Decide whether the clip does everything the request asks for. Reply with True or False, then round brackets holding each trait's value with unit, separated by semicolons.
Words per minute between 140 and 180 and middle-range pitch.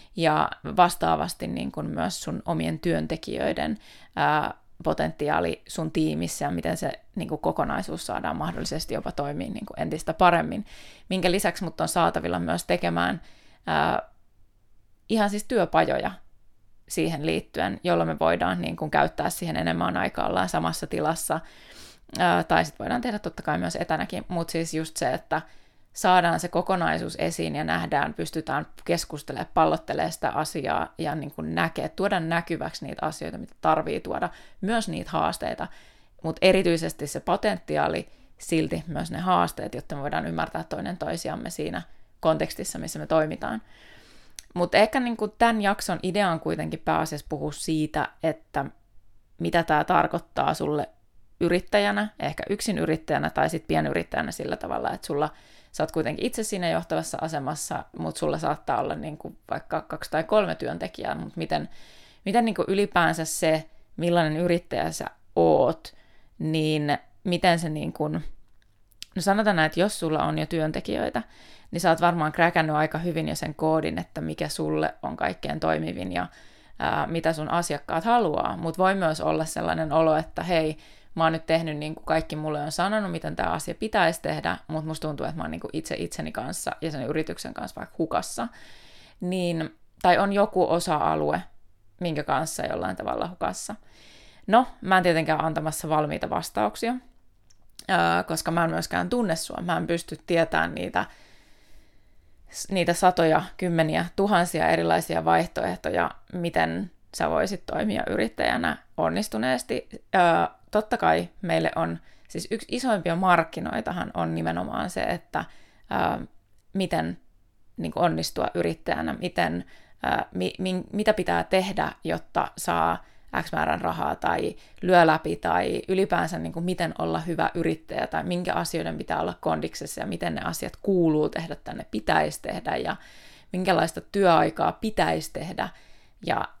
True (150 wpm; 160 Hz)